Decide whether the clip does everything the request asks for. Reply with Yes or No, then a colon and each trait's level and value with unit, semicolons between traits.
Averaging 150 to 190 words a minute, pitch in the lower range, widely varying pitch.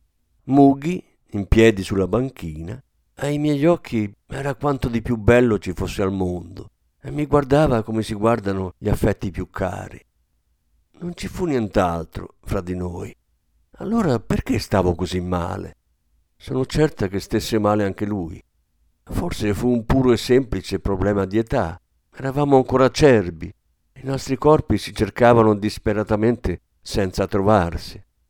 No: average, 140 wpm; low, 105 Hz; wide, 5.8 semitones